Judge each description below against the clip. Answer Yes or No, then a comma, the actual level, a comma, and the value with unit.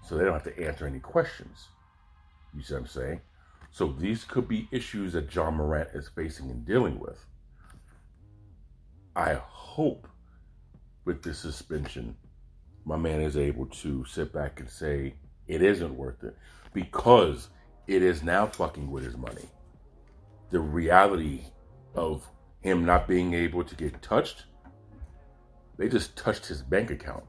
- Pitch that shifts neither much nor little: Yes, average, 3.8 semitones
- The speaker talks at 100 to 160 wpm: Yes, average, 150 wpm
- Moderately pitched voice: No, very low, 75 Hz